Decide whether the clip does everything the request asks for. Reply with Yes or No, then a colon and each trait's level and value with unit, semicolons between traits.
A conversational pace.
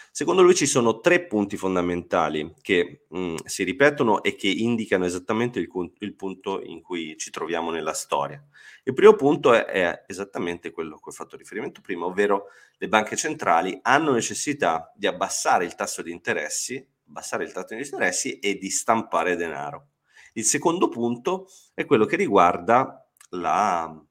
Yes: average, 160 wpm